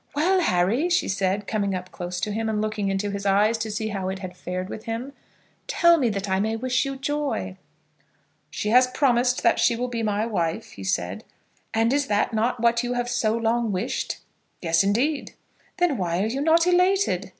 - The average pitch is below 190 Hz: No, high, 220 Hz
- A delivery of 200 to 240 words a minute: Yes, fast, 205 wpm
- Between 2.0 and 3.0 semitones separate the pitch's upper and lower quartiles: No, average, 4.4 semitones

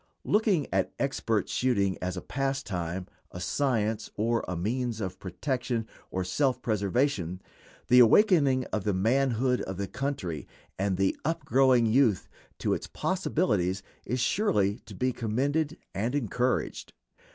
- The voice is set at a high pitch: No, low, 120 Hz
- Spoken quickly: No, average, 140 wpm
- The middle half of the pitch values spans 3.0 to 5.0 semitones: No, wide, 5.6 semitones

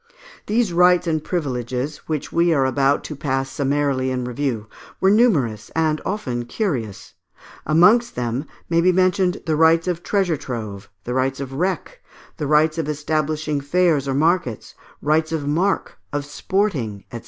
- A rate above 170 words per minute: No, average, 155 wpm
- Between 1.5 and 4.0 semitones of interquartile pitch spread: No, average, 4.7 semitones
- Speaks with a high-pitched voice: No, medium, 150 Hz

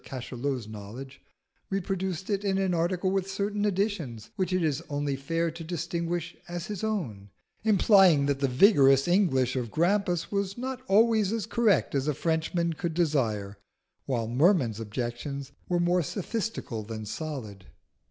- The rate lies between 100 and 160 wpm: Yes, average, 150 wpm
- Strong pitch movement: Yes, wide, 6.6 semitones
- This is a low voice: No, medium, 165 Hz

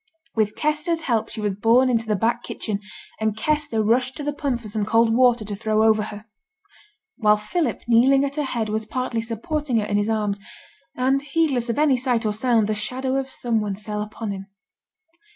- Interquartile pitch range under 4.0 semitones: Yes, average, 3.5 semitones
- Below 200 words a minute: No, fast, 205 wpm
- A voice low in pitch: No, high, 230 Hz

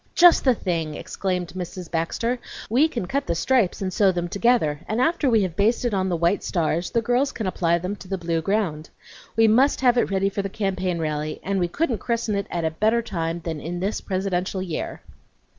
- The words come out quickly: Yes, fast, 215 wpm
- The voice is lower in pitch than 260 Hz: Yes, high, 190 Hz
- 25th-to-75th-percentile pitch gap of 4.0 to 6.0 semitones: Yes, average, 4.9 semitones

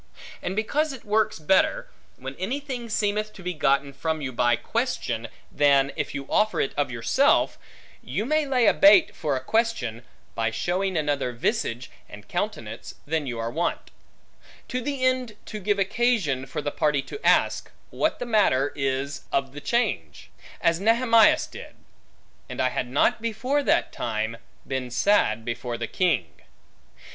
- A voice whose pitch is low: No, medium, 160 Hz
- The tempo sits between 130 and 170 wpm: Yes, average, 160 wpm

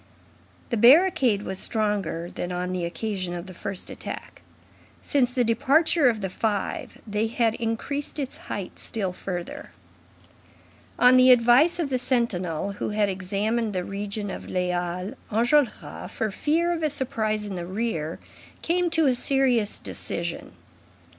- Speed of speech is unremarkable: Yes, average, 150 wpm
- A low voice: No, high, 215 Hz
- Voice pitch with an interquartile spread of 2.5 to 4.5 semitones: No, average, 5.1 semitones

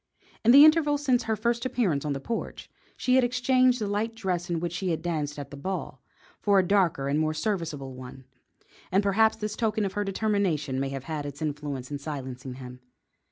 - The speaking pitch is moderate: Yes, medium, 180 Hz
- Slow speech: No, fast, 205 wpm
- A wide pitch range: Yes, wide, 7.4 semitones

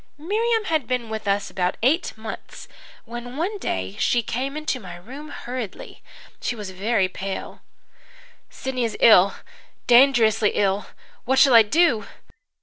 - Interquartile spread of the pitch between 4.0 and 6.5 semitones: Yes, average, 5.0 semitones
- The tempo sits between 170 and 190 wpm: No, average, 145 wpm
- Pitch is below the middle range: No, high, 235 Hz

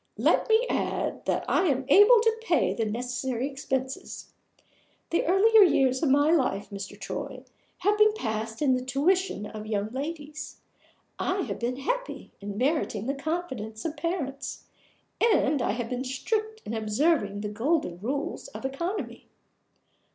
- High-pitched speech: Yes, very high, 275 Hz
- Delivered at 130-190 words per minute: Yes, average, 150 wpm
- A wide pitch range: Yes, wide, 7.1 semitones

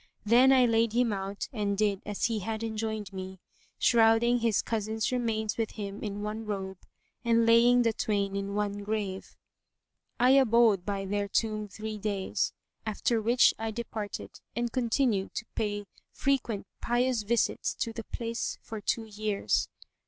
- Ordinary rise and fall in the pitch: No, narrow, 2.2 semitones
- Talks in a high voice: Yes, high, 220 Hz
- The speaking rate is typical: Yes, average, 155 wpm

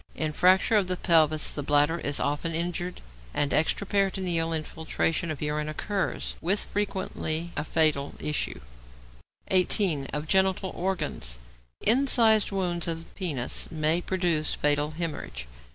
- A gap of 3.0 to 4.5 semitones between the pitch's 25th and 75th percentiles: Yes, average, 3.8 semitones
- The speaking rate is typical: No, slow, 125 wpm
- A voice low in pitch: No, medium, 165 Hz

